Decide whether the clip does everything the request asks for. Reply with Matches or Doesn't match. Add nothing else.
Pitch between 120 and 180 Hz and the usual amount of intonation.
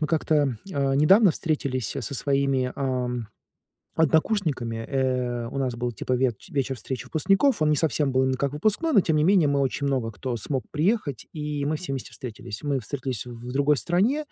Matches